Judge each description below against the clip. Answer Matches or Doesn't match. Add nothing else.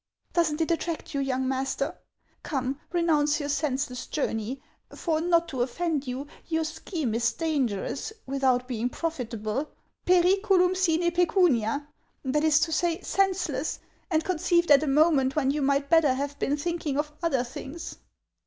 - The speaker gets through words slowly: Doesn't match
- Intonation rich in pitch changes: Doesn't match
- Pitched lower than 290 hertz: Doesn't match